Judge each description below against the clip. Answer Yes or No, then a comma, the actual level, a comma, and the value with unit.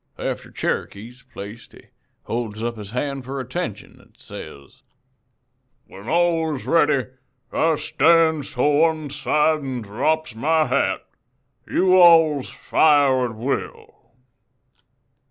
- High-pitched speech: No, medium, 140 Hz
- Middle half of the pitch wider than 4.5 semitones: Yes, average, 4.9 semitones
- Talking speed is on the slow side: Yes, slow, 120 wpm